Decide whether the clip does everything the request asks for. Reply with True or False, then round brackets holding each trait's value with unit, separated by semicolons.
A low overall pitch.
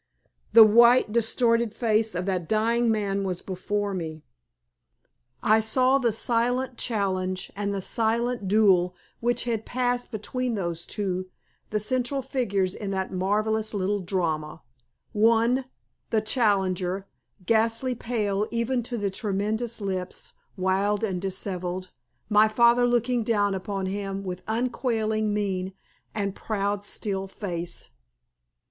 False (210 Hz)